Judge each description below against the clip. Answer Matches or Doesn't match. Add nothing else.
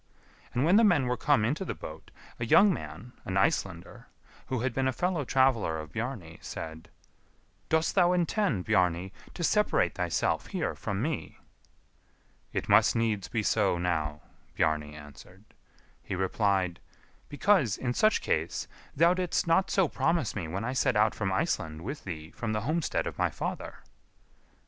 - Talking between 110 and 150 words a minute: Doesn't match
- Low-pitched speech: Matches